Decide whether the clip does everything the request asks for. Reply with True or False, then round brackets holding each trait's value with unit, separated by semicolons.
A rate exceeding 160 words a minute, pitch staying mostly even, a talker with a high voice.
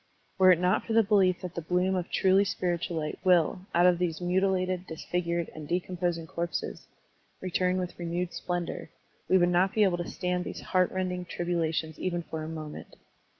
False (190 wpm; 1.3 semitones; 180 Hz)